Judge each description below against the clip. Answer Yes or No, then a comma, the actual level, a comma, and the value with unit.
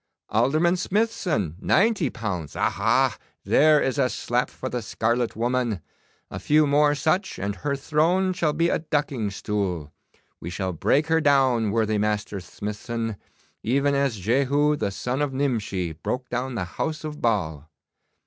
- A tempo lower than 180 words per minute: Yes, average, 150 wpm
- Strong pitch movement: Yes, wide, 6.1 semitones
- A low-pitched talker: Yes, low, 125 Hz